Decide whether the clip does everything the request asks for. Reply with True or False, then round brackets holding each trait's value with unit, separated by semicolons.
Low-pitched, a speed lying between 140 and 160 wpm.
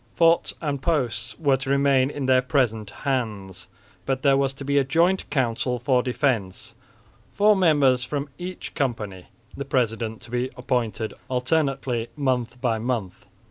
True (130 Hz; 150 wpm)